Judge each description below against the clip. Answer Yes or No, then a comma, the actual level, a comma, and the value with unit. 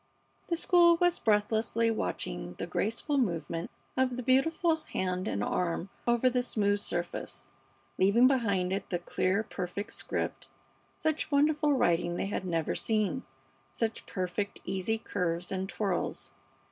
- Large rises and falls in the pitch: Yes, wide, 5.9 semitones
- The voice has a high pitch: Yes, high, 210 Hz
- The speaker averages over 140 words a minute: No, slow, 135 wpm